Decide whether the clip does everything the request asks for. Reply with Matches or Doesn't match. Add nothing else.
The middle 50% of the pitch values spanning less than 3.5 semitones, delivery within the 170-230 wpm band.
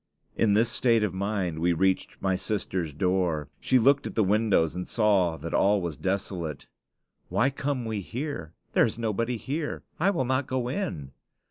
Doesn't match